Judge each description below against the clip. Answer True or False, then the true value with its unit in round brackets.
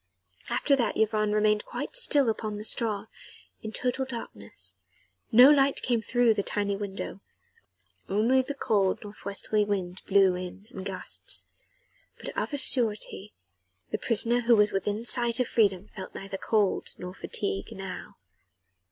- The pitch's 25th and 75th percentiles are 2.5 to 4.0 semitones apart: True (3.4 semitones)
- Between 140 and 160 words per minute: True (150 wpm)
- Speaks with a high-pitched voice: True (210 Hz)